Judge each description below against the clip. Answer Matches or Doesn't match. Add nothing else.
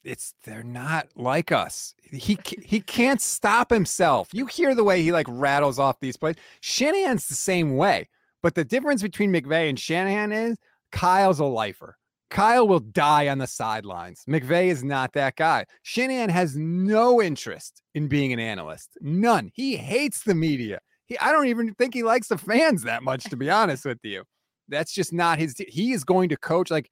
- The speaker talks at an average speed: Matches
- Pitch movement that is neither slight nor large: Doesn't match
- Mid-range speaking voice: Matches